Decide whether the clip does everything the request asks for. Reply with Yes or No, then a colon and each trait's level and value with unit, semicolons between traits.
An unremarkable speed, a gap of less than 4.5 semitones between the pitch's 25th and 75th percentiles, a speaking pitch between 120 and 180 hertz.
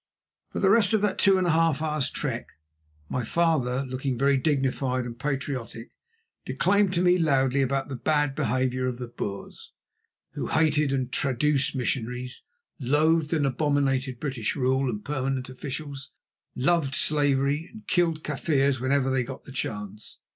Yes: average, 155 wpm; average, 3.0 semitones; low, 135 Hz